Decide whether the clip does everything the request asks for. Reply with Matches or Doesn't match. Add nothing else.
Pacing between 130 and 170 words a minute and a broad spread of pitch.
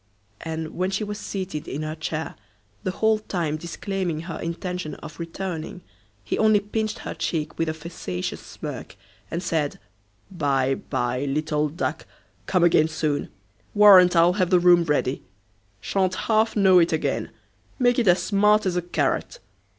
Doesn't match